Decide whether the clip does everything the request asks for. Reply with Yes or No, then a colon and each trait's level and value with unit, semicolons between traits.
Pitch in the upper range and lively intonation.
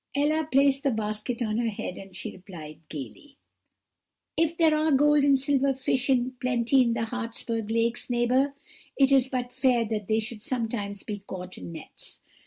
No: high, 245 Hz; average, 4.1 semitones